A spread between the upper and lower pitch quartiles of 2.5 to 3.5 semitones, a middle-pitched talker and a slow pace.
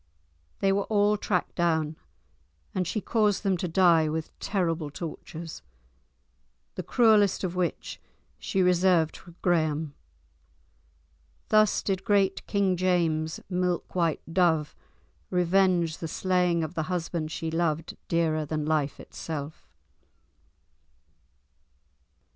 Yes: average, 2.9 semitones; medium, 175 Hz; slow, 115 wpm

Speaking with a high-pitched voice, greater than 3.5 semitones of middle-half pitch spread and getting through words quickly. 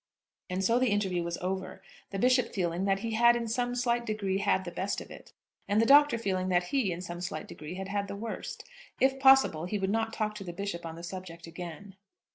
Yes: high, 195 Hz; average, 4.1 semitones; fast, 235 wpm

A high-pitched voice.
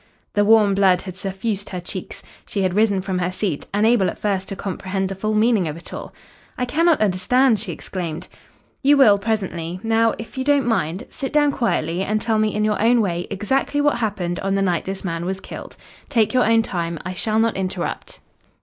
Yes: high, 200 Hz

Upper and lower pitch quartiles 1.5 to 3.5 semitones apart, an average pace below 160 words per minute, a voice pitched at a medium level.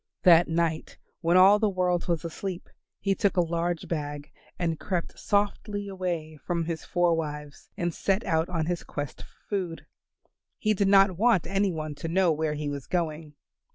No: average, 3.1 semitones; average, 180 wpm; medium, 170 Hz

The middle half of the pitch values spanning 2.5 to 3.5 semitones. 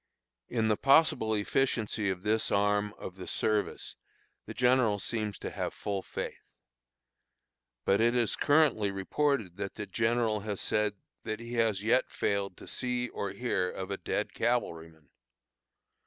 Yes: average, 3.0 semitones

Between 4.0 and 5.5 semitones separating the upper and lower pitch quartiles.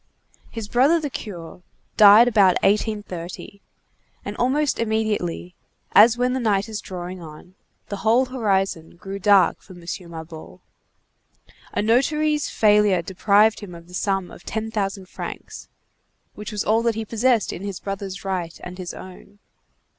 No: average, 3.4 semitones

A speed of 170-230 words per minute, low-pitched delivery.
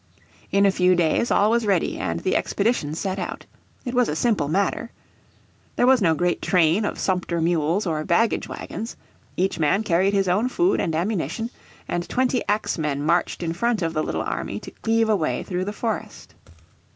No: average, 190 wpm; medium, 185 Hz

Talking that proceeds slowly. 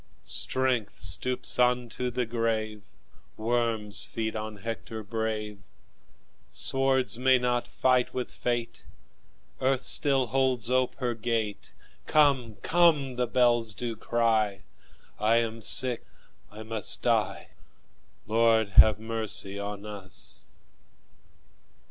Yes: slow, 105 wpm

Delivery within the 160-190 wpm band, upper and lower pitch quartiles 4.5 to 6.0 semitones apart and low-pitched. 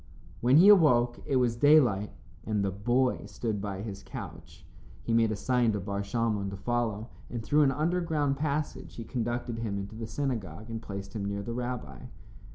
No: average, 185 wpm; average, 4.0 semitones; low, 115 Hz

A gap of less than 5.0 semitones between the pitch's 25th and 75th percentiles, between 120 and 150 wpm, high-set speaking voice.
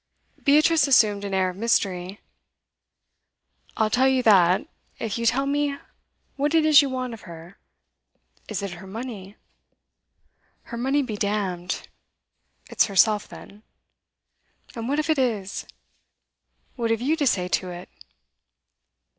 No: wide, 5.6 semitones; average, 140 wpm; high, 225 Hz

